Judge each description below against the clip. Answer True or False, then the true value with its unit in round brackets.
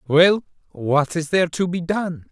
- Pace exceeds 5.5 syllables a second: False (4.3 syllables/s)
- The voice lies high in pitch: False (170 Hz)